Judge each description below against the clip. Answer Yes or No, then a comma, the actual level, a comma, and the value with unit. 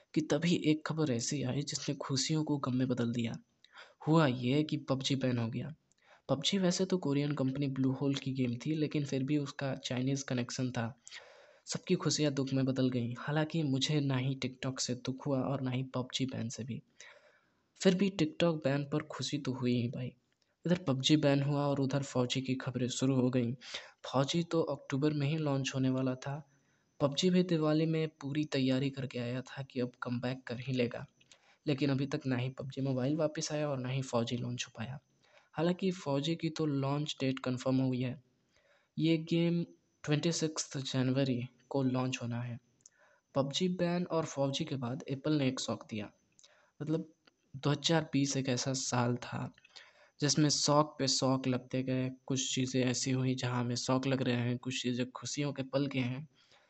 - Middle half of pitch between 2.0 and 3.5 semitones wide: Yes, average, 2.7 semitones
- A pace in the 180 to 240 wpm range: Yes, average, 185 wpm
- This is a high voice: No, low, 135 Hz